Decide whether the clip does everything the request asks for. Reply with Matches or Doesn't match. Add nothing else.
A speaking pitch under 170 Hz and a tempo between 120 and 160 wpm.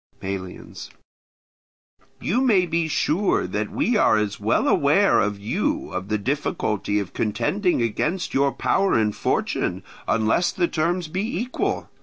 Matches